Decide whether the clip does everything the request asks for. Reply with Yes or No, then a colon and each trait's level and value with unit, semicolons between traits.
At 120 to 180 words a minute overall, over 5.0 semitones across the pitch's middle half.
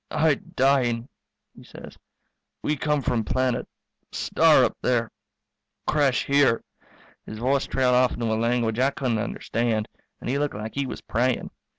No: average, 160 wpm; average, 3.0 semitones